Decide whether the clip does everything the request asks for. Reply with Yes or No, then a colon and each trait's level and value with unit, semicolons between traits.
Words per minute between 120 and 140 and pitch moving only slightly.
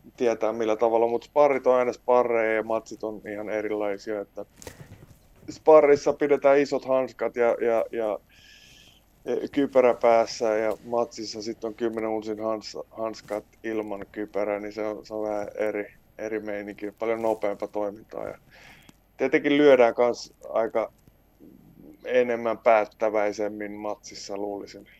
Yes: average, 130 wpm; narrow, 2.0 semitones